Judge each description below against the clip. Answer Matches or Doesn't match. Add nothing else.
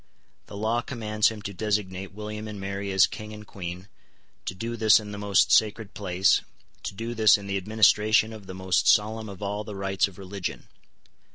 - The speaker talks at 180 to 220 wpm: Matches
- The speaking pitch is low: Matches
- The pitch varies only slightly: Matches